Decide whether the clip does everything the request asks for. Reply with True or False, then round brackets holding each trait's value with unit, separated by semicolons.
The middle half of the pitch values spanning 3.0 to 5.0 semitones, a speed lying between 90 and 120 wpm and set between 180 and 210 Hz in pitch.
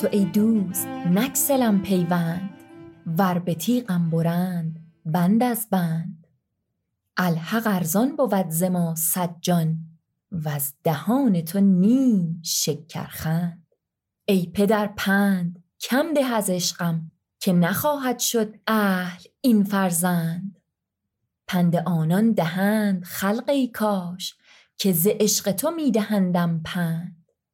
True (3.8 semitones; 105 wpm; 185 Hz)